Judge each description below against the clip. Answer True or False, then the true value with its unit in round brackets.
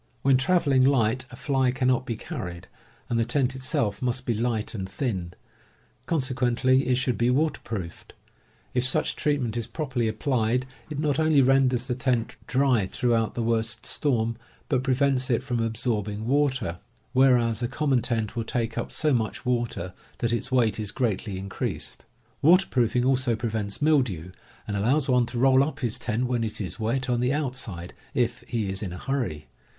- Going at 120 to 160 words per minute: False (175 wpm)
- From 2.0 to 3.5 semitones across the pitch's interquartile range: True (2.9 semitones)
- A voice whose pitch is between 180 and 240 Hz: False (125 Hz)